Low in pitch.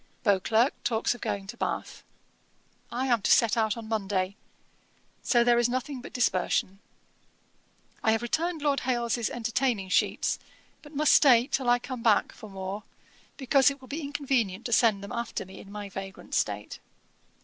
No: high, 235 Hz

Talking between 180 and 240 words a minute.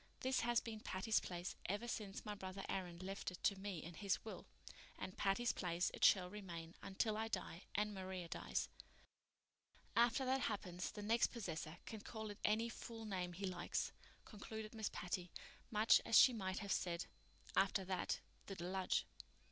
No: average, 170 wpm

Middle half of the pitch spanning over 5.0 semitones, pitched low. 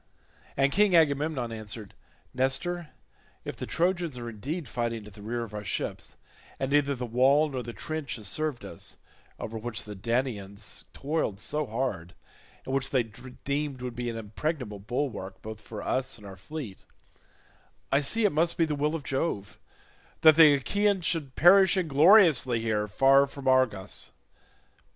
Yes: wide, 5.4 semitones; low, 130 Hz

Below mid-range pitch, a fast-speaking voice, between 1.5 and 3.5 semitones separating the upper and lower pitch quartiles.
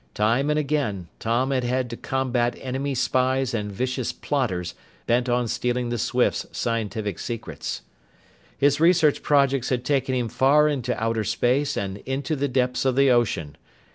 No: low, 125 Hz; average, 160 wpm; average, 2.8 semitones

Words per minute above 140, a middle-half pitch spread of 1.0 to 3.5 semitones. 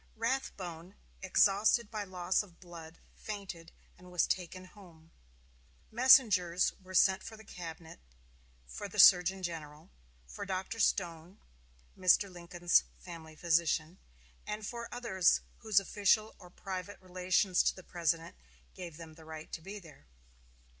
No: slow, 135 wpm; average, 3.1 semitones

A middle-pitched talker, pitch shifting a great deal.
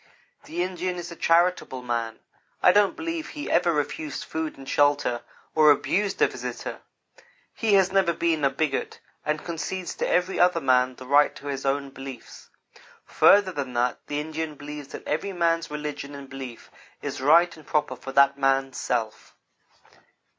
No: medium, 150 Hz; average, 4.2 semitones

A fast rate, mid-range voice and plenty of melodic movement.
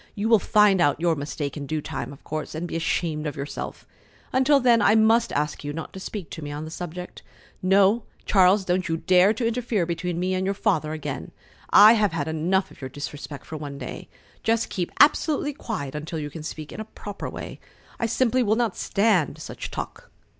Yes: fast, 210 wpm; medium, 180 Hz; wide, 5.7 semitones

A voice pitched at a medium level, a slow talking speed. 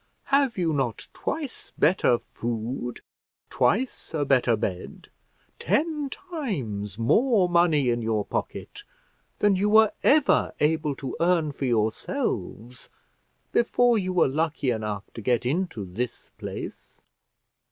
Yes: medium, 150 Hz; slow, 120 wpm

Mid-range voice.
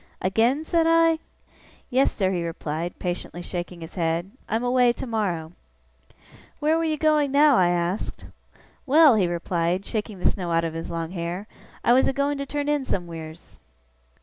No: high, 195 Hz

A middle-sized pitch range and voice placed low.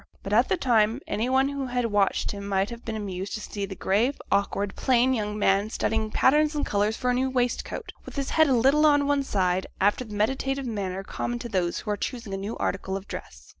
No: average, 4.6 semitones; high, 220 Hz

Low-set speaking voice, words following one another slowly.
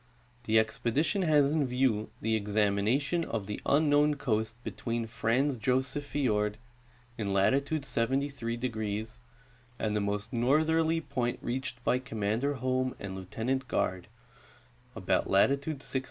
Yes: low, 125 Hz; slow, 125 wpm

